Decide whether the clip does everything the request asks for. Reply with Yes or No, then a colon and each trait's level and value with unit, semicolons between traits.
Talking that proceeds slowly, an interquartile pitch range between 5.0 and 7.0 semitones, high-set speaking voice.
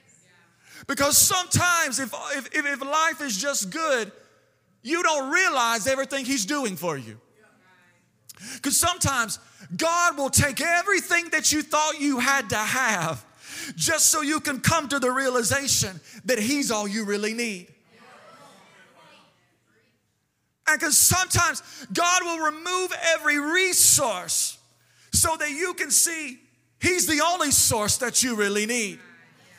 Yes: slow, 130 wpm; wide, 5.5 semitones; very high, 280 Hz